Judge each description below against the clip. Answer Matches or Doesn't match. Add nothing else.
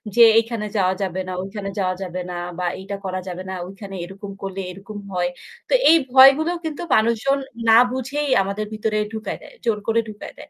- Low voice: Doesn't match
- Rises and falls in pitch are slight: Doesn't match